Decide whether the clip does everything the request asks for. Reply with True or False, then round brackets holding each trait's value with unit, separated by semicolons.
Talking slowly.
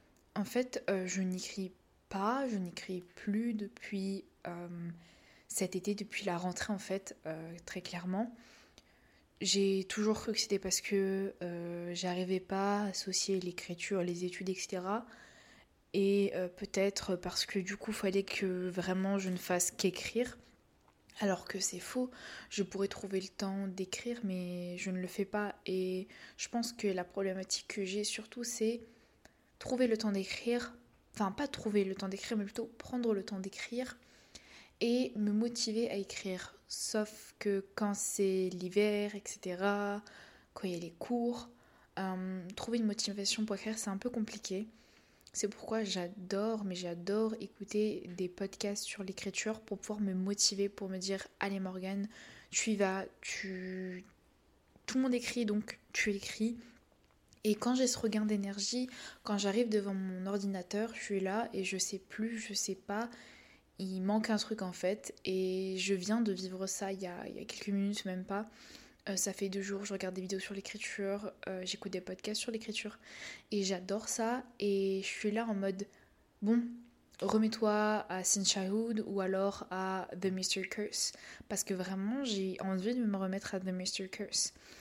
False (170 wpm)